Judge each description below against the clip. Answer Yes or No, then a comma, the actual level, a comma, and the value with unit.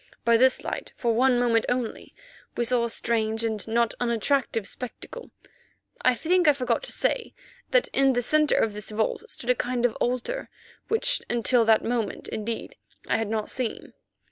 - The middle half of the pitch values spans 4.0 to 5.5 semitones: No, narrow, 2.5 semitones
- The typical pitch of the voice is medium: No, high, 240 Hz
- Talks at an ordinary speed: Yes, average, 175 wpm